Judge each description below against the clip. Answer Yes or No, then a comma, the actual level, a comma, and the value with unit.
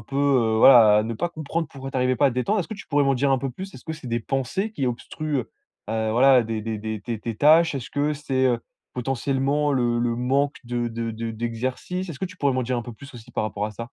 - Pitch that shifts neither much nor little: Yes, average, 3.5 semitones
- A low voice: Yes, low, 130 Hz